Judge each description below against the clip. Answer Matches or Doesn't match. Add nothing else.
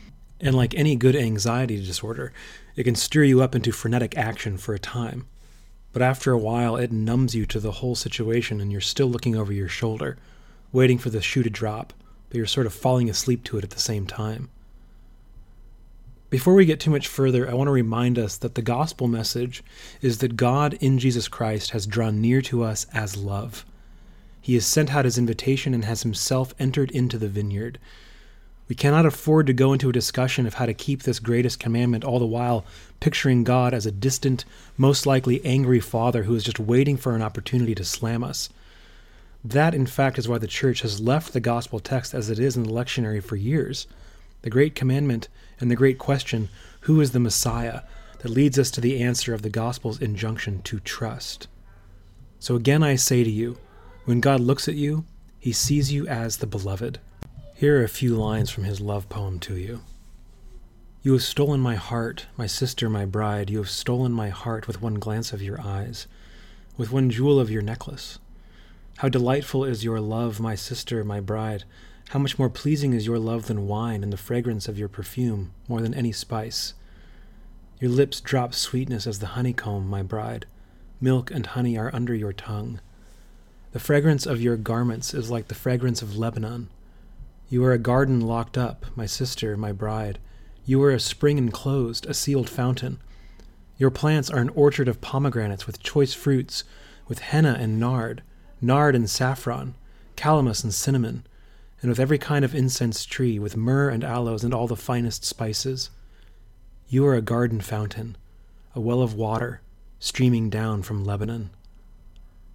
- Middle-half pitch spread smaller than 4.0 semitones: Matches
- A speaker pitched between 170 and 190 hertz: Doesn't match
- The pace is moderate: Matches